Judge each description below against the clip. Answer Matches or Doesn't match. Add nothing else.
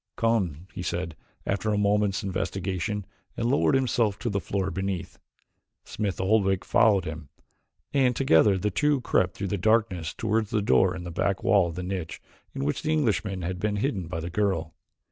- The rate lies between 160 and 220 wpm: Matches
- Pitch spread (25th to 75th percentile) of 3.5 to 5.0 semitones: Doesn't match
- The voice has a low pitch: Matches